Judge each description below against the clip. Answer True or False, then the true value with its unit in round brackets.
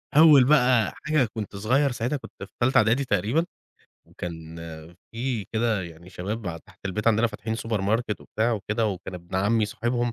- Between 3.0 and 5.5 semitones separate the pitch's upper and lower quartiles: True (3.5 semitones)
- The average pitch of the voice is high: False (110 Hz)